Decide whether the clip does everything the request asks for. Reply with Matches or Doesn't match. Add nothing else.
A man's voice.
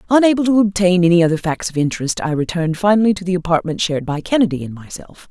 Doesn't match